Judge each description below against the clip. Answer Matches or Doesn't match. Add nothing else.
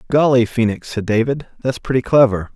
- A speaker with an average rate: Matches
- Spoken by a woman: Doesn't match